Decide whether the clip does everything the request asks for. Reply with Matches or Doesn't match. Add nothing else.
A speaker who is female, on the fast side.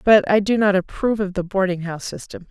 Matches